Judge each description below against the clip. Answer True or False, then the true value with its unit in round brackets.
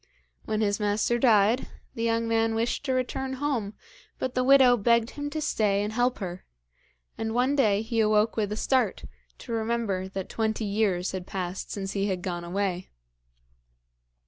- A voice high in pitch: True (220 Hz)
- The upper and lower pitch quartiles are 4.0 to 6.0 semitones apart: False (3.2 semitones)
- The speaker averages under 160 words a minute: False (170 wpm)